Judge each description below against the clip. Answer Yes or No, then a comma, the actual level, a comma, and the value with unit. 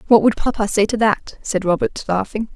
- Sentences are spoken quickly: Yes, fast, 210 wpm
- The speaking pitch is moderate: No, high, 210 Hz